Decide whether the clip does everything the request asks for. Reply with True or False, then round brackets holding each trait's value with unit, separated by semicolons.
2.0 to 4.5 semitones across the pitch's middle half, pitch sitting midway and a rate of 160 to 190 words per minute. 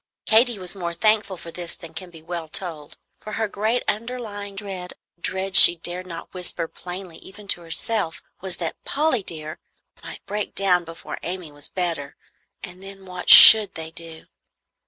True (3.3 semitones; 180 Hz; 175 wpm)